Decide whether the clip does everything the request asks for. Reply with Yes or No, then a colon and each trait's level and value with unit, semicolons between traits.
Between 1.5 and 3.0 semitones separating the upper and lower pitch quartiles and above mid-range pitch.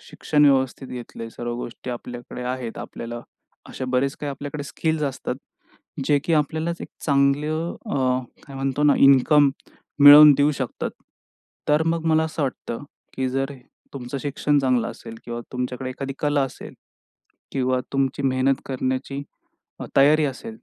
No: narrow, 2.4 semitones; low, 135 Hz